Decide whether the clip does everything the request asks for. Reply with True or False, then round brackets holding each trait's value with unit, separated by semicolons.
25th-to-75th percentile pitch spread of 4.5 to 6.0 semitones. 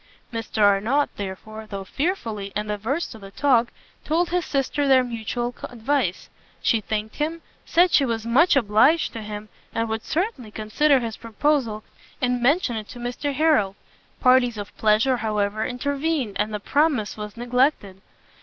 True (4.9 semitones)